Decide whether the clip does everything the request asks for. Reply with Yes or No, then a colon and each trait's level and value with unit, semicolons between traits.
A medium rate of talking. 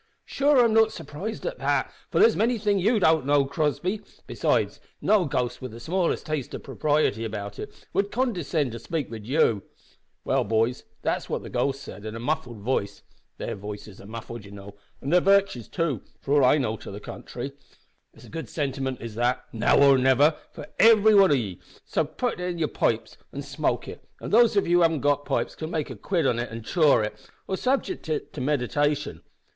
No: fast, 215 wpm